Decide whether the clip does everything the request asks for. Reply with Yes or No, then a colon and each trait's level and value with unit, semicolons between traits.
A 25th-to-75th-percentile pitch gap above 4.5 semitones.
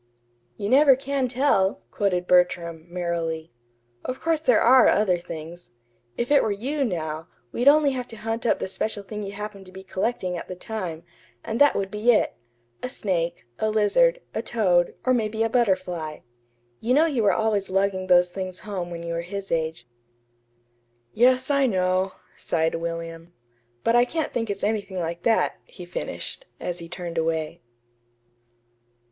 Yes: wide, 5.4 semitones